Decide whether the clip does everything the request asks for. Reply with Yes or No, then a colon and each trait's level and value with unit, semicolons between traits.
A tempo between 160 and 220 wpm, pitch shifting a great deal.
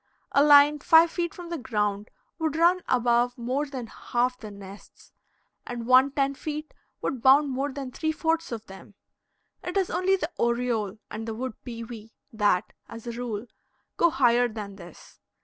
No: average, 170 wpm; average, 4.9 semitones